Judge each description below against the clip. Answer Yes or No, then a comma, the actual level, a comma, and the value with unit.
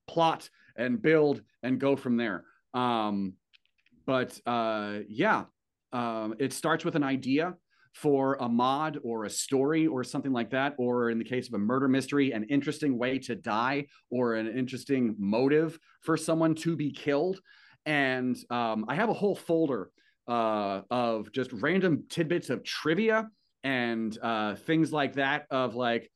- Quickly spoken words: No, average, 160 wpm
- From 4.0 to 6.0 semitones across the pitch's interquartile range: Yes, average, 4.4 semitones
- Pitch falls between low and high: No, low, 130 Hz